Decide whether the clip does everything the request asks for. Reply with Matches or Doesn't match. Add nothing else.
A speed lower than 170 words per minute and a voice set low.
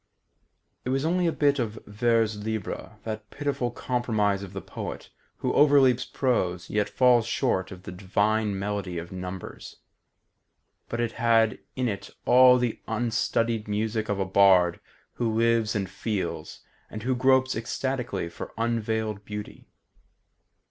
Matches